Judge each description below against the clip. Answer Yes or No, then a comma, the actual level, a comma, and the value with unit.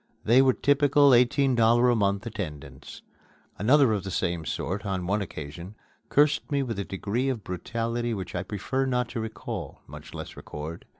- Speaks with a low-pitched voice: Yes, low, 110 Hz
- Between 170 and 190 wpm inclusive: Yes, average, 175 wpm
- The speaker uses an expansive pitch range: No, average, 4.9 semitones